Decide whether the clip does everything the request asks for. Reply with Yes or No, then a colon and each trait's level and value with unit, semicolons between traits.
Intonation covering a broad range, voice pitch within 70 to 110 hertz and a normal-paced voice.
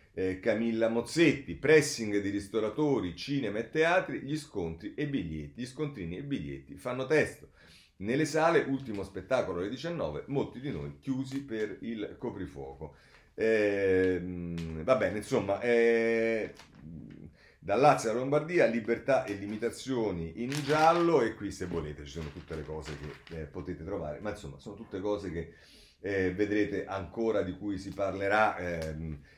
Yes: wide, 5.9 semitones; low, 100 Hz; average, 150 wpm